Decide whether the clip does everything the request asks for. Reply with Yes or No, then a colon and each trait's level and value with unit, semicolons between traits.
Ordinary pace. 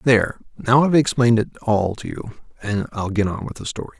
No: fast, 225 wpm